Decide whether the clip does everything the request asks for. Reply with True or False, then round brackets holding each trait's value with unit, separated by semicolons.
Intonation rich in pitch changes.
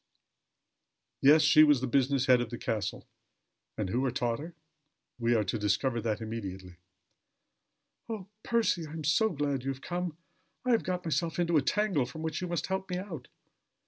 True (6.4 semitones)